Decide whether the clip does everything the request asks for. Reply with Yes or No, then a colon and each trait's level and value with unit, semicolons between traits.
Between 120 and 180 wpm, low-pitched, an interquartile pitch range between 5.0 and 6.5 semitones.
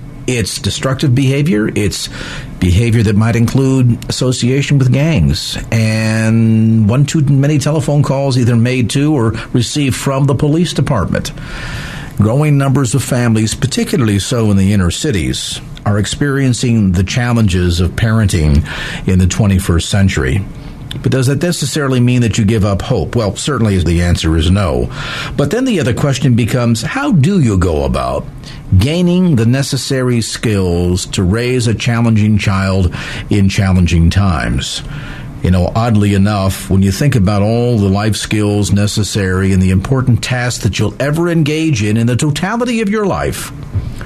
Yes: average, 155 wpm; low, 115 Hz; wide, 5.5 semitones